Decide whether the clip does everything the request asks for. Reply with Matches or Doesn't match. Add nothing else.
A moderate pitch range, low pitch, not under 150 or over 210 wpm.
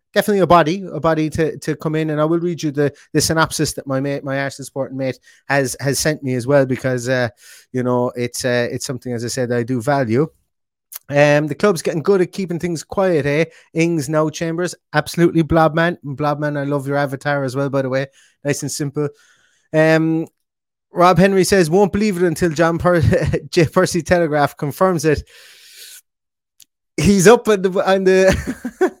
Doesn't match